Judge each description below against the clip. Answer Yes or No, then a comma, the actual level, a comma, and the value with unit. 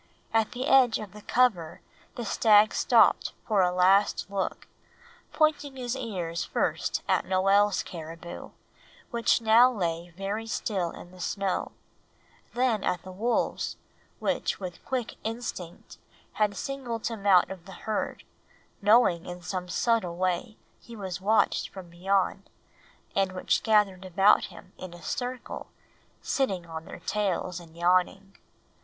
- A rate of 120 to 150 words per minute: Yes, average, 140 wpm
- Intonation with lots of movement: No, average, 3.9 semitones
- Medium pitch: No, high, 195 Hz